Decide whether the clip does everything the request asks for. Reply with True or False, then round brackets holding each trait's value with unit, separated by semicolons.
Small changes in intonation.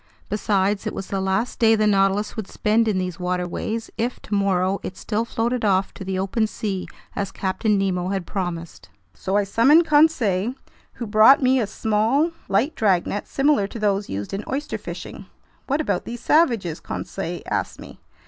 False (3.2 semitones)